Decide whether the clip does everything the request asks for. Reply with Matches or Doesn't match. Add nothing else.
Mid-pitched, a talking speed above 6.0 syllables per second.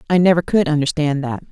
Matches